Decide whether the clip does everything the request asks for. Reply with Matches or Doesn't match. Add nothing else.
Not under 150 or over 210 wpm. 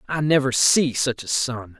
Matches